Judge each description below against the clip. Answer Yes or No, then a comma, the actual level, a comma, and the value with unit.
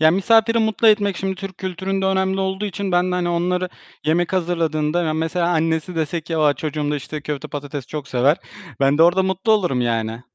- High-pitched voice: No, medium, 175 Hz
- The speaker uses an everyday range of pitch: Yes, average, 3.8 semitones